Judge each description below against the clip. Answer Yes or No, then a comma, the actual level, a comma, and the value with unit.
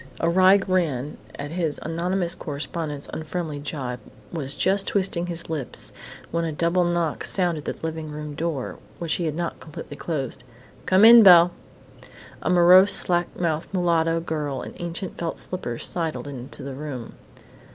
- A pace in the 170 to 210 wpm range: No, average, 160 wpm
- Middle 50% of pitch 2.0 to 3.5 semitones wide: Yes, average, 3.0 semitones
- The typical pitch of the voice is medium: Yes, medium, 165 Hz